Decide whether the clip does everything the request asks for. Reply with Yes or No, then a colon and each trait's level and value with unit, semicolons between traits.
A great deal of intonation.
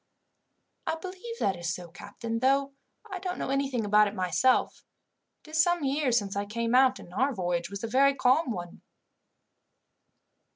Yes: wide, 5.7 semitones